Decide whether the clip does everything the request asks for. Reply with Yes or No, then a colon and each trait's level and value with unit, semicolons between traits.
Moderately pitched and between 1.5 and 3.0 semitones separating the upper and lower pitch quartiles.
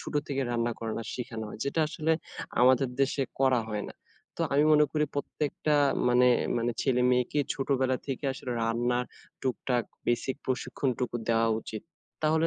No: low, 125 Hz; narrow, 2.5 semitones